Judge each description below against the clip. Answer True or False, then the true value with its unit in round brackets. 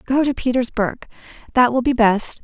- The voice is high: True (245 Hz)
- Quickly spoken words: False (175 wpm)